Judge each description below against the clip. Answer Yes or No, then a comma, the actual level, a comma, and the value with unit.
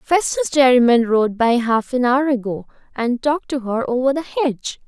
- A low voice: No, very high, 255 Hz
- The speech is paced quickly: No, average, 185 wpm